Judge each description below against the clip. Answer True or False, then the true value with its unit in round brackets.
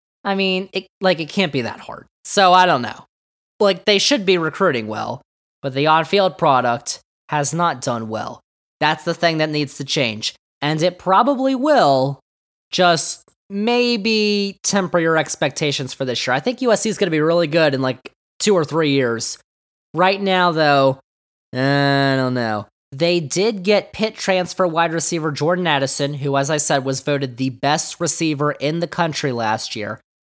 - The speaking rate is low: False (180 wpm)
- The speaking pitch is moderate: True (160 Hz)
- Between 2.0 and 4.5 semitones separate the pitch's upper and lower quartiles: False (5.2 semitones)